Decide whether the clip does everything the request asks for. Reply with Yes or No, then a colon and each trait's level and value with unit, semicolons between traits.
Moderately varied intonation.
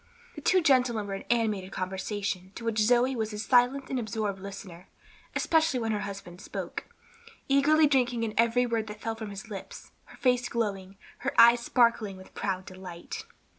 Yes: average, 3.9 semitones